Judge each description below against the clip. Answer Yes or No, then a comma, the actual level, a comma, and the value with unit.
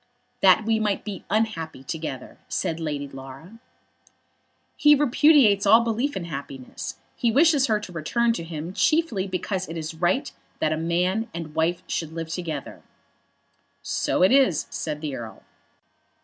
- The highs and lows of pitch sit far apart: Yes, wide, 6.0 semitones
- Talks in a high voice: No, medium, 180 Hz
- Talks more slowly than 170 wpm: Yes, average, 150 wpm